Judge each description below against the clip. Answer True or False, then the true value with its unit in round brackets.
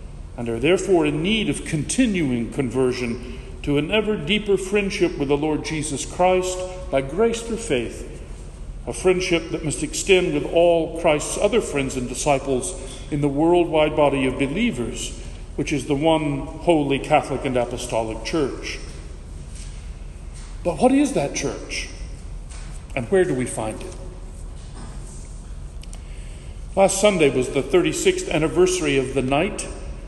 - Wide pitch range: True (7.2 semitones)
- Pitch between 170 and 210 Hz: False (145 Hz)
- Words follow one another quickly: False (140 wpm)